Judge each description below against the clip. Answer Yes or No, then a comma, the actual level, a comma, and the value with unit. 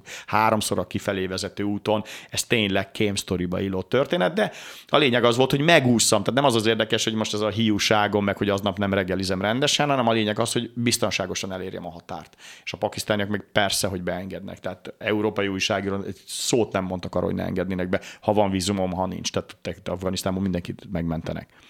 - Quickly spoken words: Yes, fast, 195 wpm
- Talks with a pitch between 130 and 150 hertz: No, low, 100 Hz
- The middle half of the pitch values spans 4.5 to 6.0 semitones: No, average, 2.7 semitones